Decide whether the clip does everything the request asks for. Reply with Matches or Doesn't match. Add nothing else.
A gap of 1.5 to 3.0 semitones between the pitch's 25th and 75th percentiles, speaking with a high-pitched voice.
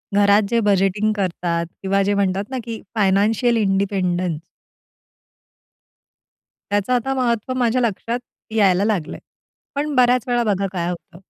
Doesn't match